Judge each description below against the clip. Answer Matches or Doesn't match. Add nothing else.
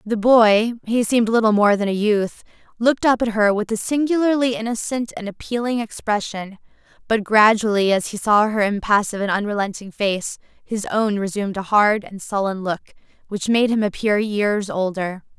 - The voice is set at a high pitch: Matches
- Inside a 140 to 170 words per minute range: Matches